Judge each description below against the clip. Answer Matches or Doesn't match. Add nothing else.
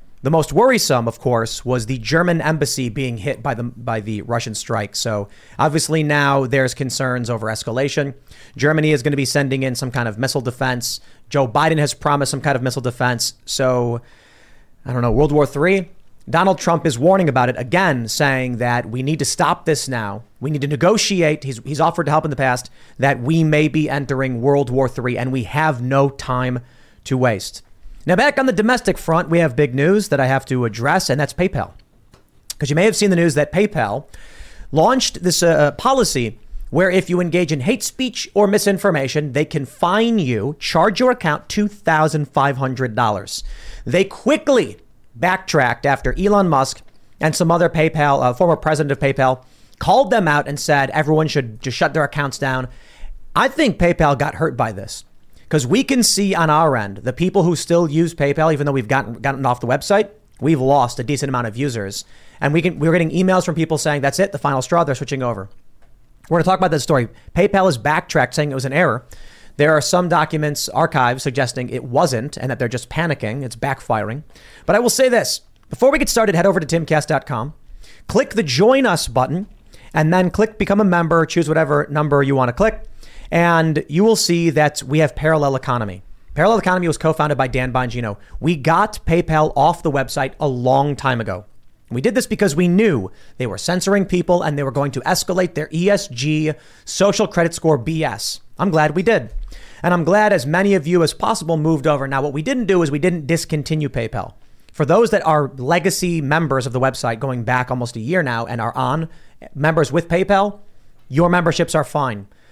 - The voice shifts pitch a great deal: Doesn't match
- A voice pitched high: Doesn't match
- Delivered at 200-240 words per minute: Matches